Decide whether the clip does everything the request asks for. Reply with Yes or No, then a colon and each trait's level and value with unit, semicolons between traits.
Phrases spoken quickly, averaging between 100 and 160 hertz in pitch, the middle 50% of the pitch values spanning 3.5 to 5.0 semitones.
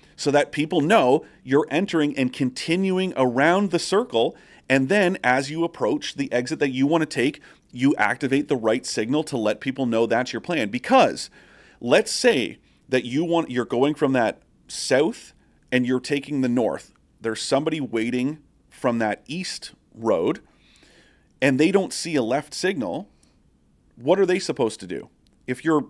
No: average, 170 wpm; medium, 140 Hz; average, 4.2 semitones